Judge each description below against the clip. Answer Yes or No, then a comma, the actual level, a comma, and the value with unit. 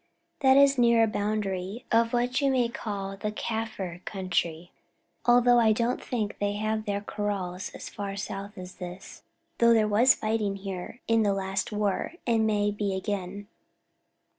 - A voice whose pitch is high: Yes, high, 210 Hz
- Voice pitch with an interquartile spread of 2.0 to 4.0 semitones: Yes, average, 2.7 semitones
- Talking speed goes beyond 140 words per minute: Yes, average, 165 wpm